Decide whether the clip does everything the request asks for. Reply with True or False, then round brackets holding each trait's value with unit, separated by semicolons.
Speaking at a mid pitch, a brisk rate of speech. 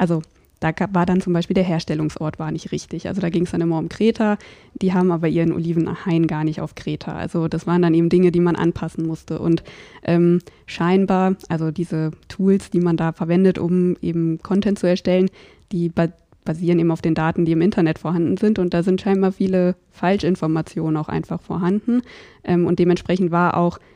True (175 Hz; 200 wpm)